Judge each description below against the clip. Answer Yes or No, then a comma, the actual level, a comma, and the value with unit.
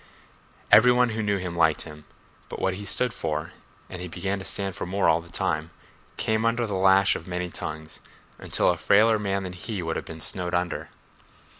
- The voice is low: Yes, very low, 95 Hz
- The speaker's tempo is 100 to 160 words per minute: No, average, 200 wpm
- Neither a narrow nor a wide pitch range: Yes, average, 3.4 semitones